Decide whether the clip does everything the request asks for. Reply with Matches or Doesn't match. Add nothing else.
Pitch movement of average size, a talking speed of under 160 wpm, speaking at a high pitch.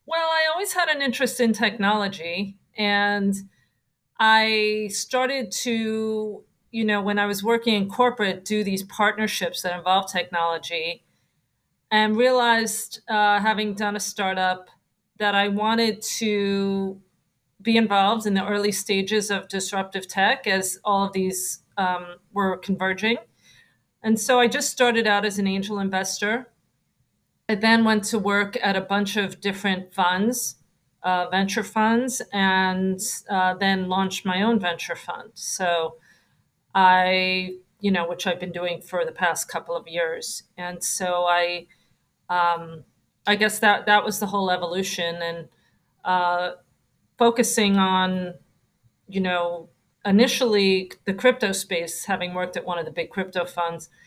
Matches